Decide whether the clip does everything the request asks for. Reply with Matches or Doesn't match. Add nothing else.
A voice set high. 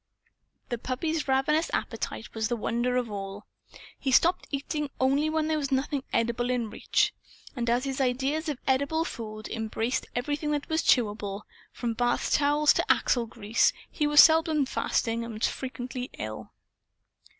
Matches